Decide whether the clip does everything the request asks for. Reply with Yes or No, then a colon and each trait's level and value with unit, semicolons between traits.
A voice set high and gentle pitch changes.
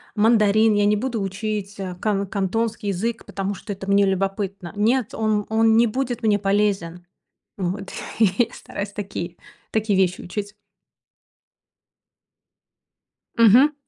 Yes: high, 205 Hz; narrow, 2.2 semitones